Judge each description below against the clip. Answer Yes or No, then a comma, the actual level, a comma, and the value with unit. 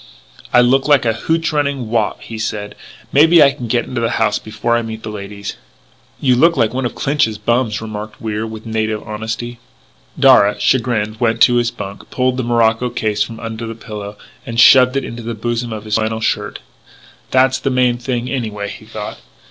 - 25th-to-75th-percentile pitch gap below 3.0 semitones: Yes, narrow, 2.6 semitones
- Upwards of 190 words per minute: Yes, average, 200 wpm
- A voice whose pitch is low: Yes, low, 115 Hz